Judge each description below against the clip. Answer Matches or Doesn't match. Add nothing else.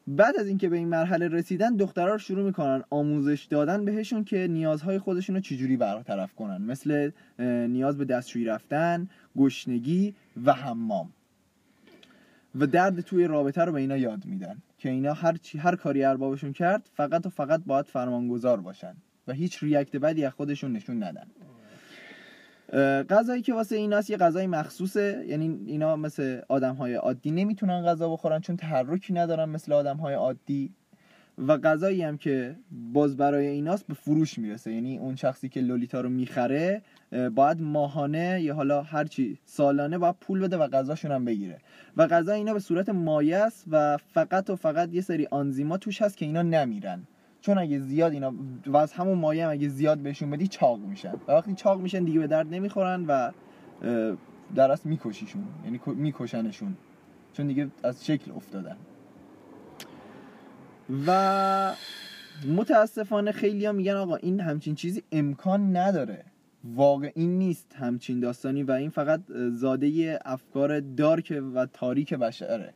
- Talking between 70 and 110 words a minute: Doesn't match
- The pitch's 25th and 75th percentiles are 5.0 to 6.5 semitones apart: Matches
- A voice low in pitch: Doesn't match